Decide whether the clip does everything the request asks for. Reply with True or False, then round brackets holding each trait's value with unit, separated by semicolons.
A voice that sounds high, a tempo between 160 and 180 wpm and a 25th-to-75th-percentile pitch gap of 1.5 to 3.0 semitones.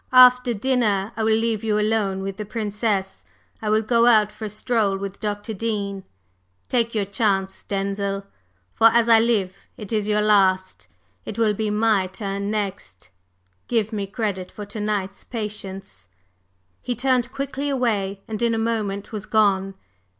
True (210 Hz; 165 wpm; 2.4 semitones)